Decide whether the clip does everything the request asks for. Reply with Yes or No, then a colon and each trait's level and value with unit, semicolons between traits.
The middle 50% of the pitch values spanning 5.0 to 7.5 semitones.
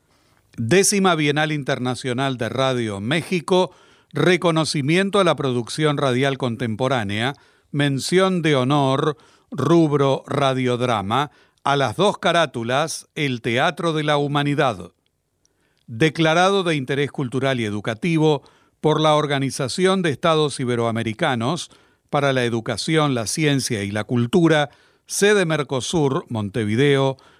No: average, 4.0 semitones